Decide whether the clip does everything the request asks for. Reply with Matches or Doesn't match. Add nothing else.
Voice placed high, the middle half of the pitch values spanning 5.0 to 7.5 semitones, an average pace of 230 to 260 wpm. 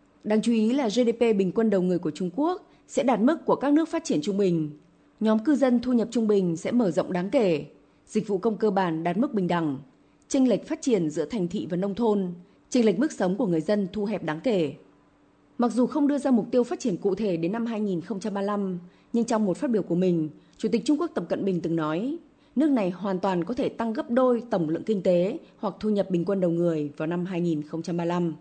Matches